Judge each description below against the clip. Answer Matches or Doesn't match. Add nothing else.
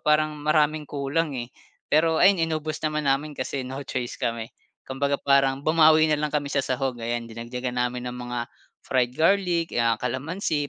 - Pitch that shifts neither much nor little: Matches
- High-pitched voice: Doesn't match